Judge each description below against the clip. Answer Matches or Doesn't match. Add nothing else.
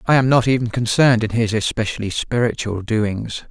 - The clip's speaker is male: Matches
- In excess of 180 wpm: Doesn't match